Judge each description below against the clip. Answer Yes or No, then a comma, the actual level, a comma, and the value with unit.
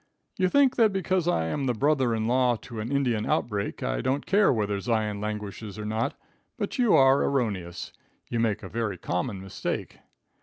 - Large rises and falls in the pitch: No, average, 4.8 semitones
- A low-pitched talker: Yes, low, 115 Hz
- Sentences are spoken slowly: No, average, 185 wpm